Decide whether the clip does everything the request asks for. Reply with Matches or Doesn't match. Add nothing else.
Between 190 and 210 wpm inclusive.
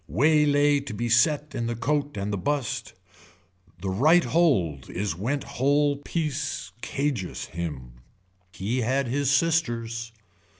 Doesn't match